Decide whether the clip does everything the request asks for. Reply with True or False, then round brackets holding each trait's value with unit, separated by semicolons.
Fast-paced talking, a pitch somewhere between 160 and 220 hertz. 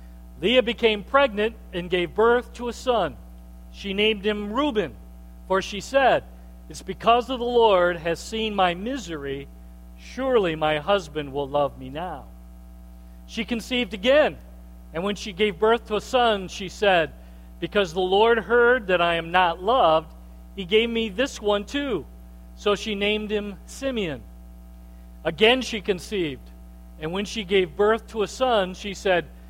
False (160 wpm; 190 Hz)